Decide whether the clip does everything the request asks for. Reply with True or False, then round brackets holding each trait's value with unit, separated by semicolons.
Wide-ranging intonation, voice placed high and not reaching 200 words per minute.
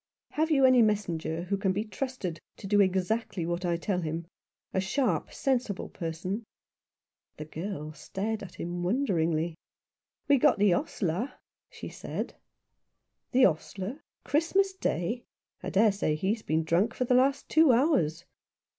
True (6.5 semitones; 195 Hz; 155 wpm)